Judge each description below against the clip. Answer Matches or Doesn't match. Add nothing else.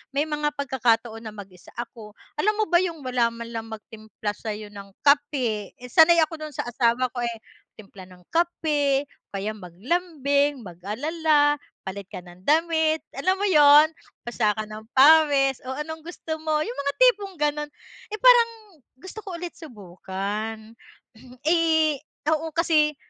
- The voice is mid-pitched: Doesn't match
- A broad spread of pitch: Matches